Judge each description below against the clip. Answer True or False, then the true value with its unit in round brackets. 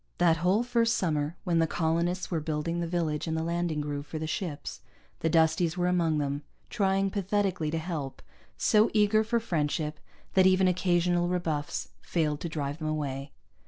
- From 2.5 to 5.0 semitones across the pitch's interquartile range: True (3.0 semitones)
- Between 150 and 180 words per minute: True (175 wpm)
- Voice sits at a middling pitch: True (170 Hz)